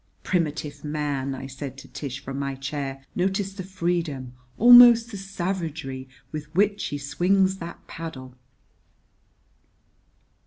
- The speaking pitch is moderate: Yes, medium, 155 Hz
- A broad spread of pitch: Yes, wide, 5.8 semitones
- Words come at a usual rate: No, slow, 120 wpm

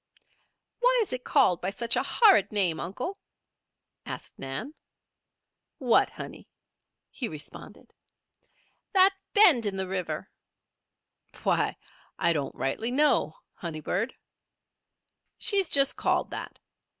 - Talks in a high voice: Yes, high, 225 Hz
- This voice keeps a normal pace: No, slow, 115 wpm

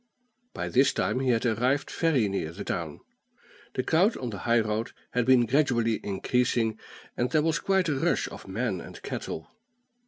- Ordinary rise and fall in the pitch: Yes, average, 3.7 semitones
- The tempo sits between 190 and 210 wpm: No, average, 180 wpm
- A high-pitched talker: No, low, 120 Hz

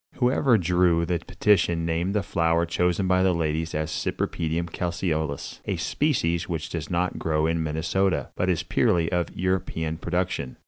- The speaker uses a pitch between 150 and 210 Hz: No, very low, 85 Hz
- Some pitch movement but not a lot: No, narrow, 2.1 semitones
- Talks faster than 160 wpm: No, average, 155 wpm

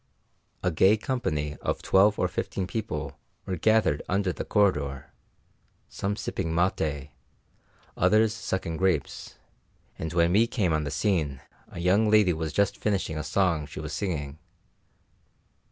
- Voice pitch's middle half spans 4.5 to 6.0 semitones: Yes, average, 4.8 semitones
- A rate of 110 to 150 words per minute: Yes, average, 140 wpm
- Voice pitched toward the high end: No, very low, 90 Hz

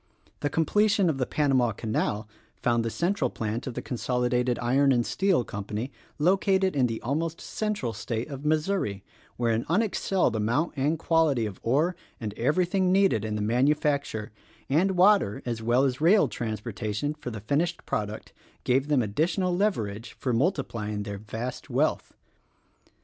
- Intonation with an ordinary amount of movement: No, wide, 6.7 semitones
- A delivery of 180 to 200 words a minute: No, average, 155 wpm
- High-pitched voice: No, low, 130 Hz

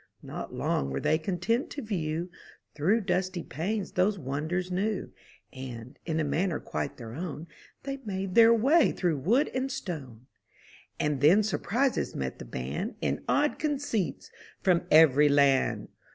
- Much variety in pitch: Yes, wide, 6.9 semitones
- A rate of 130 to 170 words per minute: Yes, average, 150 wpm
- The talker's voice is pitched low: No, medium, 180 Hz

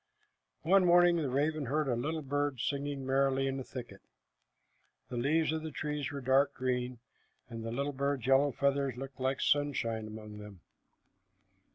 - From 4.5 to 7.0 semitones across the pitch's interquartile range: No, narrow, 2.4 semitones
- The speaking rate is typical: Yes, average, 165 wpm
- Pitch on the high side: No, low, 135 Hz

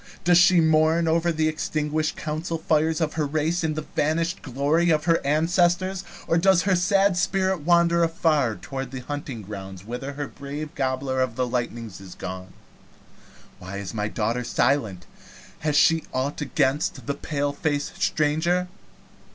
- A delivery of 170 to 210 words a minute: No, average, 155 wpm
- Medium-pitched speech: Yes, medium, 150 Hz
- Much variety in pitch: No, average, 4.2 semitones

